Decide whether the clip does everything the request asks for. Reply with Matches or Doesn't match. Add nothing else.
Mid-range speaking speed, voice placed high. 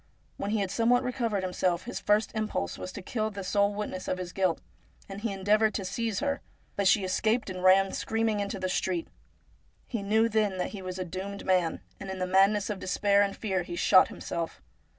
Doesn't match